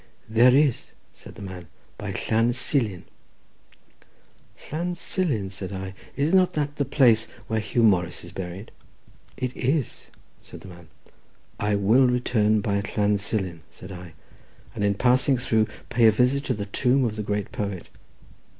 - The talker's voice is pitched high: No, low, 110 Hz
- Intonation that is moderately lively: Yes, average, 4.3 semitones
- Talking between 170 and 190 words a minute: No, average, 160 wpm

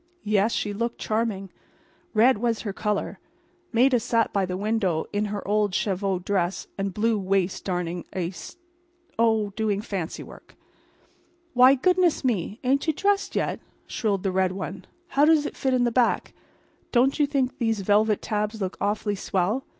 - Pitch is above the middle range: Yes, high, 210 Hz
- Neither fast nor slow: Yes, average, 165 wpm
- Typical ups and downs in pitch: Yes, average, 3.7 semitones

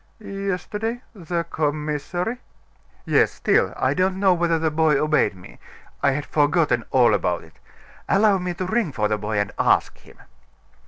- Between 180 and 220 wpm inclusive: No, average, 160 wpm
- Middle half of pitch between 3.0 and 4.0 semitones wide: No, average, 4.8 semitones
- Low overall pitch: No, medium, 165 Hz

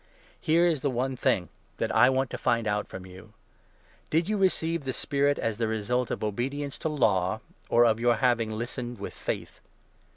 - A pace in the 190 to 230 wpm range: Yes, average, 200 wpm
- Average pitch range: Yes, average, 4.3 semitones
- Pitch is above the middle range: No, low, 120 Hz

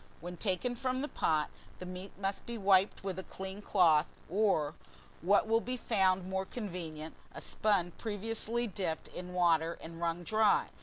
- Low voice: No, high, 190 Hz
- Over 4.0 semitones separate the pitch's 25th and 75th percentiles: No, average, 3.7 semitones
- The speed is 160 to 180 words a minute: Yes, average, 165 wpm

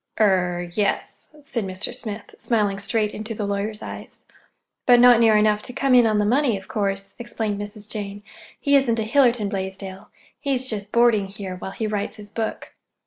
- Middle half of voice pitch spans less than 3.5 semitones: Yes, average, 2.8 semitones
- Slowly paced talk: No, average, 180 wpm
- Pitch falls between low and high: No, high, 210 Hz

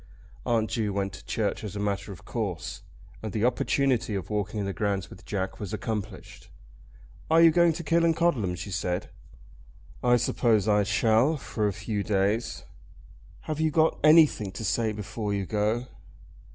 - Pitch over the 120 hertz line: No, low, 110 Hz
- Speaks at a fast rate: No, average, 165 wpm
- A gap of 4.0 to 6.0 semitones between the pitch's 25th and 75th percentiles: No, average, 3.5 semitones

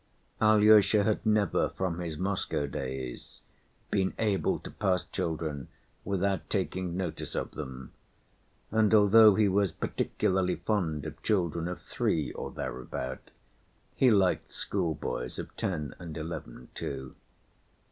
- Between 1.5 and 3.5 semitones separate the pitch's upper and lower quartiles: No, average, 4.8 semitones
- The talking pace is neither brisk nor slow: No, slow, 125 wpm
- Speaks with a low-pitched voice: Yes, very low, 90 Hz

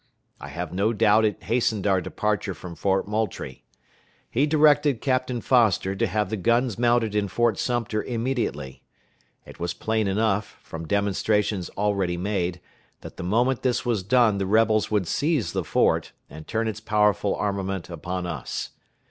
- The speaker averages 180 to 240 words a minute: No, average, 160 wpm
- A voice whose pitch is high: No, low, 105 Hz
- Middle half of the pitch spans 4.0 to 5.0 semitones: No, average, 3.4 semitones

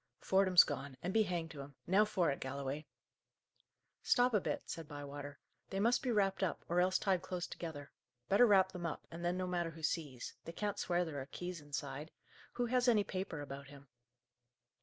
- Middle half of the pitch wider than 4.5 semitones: Yes, average, 5.1 semitones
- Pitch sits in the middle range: Yes, medium, 175 Hz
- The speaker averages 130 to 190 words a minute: No, average, 200 wpm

